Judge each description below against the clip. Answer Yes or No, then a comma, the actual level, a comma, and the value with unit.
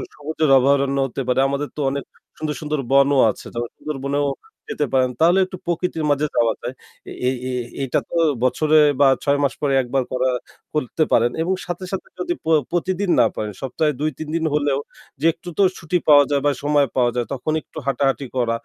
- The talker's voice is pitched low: No, medium, 145 Hz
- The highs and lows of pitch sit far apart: No, average, 2.9 semitones